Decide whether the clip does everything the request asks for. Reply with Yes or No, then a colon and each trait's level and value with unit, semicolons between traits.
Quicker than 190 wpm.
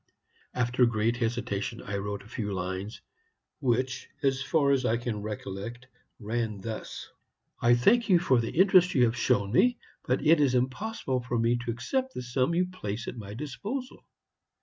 No: average, 170 wpm